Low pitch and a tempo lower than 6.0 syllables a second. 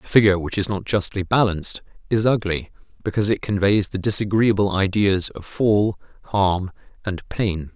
Yes: low, 100 Hz; 5.2 syllables/s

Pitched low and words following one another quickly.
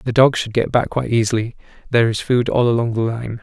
Yes: low, 115 Hz; fast, 245 wpm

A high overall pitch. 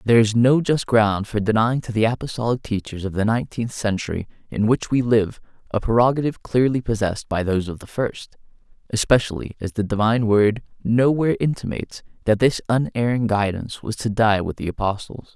No: low, 110 Hz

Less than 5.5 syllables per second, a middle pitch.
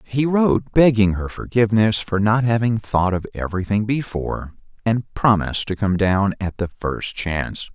No: 4.9 syllables/s; low, 105 Hz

